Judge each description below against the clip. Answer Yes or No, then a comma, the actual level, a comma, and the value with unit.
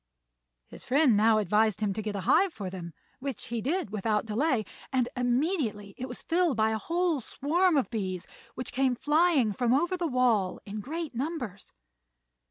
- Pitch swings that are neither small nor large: No, wide, 6.1 semitones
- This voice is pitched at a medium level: No, high, 245 Hz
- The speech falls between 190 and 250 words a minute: No, average, 180 wpm